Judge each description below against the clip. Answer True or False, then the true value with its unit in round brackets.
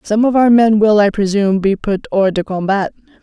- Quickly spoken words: True (225 wpm)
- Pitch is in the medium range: False (210 Hz)